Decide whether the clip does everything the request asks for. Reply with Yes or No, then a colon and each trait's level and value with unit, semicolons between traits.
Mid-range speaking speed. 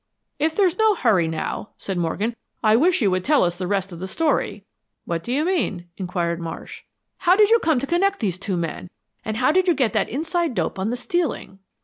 No: fast, 225 wpm